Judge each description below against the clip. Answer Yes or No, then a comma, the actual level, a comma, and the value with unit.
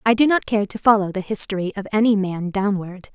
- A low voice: No, high, 205 Hz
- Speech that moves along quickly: Yes, fast, 230 wpm